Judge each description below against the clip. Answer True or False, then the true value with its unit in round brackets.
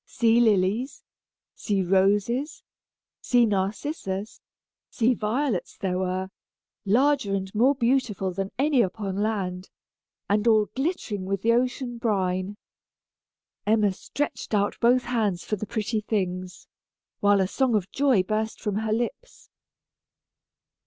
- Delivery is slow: True (125 wpm)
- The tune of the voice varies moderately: True (3.9 semitones)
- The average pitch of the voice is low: False (215 Hz)